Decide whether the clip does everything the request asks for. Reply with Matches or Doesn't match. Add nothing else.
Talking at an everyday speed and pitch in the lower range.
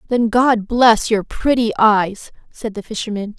Doesn't match